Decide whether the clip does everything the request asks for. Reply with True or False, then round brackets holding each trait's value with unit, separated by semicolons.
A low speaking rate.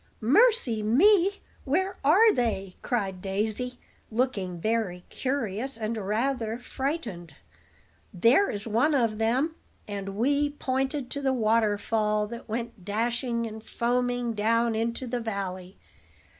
True (120 wpm)